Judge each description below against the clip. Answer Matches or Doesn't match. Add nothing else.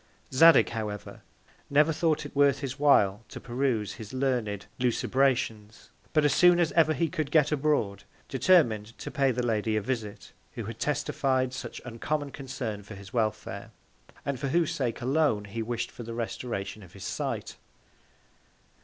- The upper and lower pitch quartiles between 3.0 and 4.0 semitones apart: Doesn't match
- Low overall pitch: Matches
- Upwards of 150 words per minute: Matches